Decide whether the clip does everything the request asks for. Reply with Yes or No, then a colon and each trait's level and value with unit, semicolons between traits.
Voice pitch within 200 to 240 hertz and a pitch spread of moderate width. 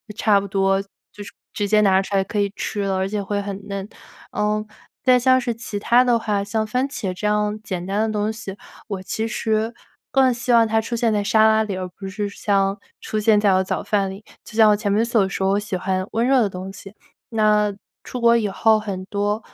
No: high, 210 Hz; narrow, 2.1 semitones